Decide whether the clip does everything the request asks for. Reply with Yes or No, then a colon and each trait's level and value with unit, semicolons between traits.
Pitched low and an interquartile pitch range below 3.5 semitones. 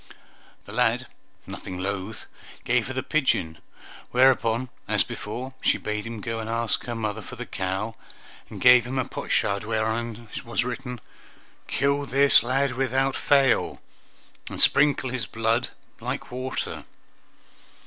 Yes: low, 120 Hz; average, 3.0 semitones